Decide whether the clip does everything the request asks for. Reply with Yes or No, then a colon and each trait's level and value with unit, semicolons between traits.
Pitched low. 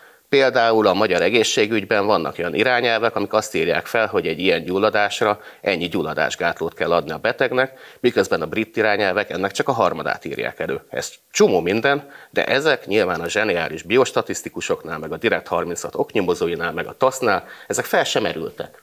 Yes: low, 115 Hz